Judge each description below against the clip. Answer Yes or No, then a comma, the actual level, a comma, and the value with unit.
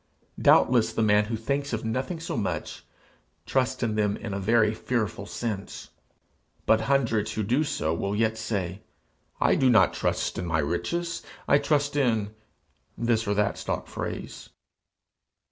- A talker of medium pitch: No, low, 110 Hz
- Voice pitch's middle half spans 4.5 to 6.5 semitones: No, average, 3.7 semitones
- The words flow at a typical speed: Yes, average, 160 wpm